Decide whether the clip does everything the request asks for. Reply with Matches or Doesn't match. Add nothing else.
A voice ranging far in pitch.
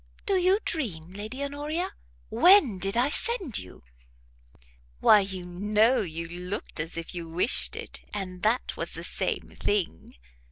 Matches